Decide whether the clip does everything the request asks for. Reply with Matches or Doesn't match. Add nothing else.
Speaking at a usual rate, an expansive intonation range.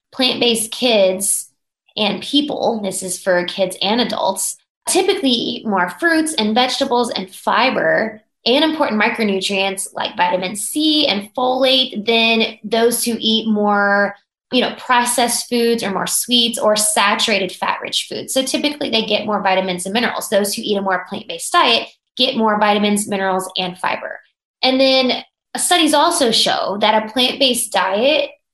Doesn't match